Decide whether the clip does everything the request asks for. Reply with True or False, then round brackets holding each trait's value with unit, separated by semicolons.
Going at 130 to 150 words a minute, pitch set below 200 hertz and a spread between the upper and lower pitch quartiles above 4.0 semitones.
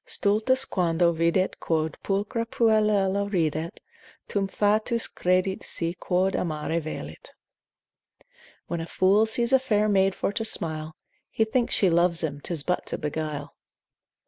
True (140 wpm; 185 Hz; 4.4 semitones)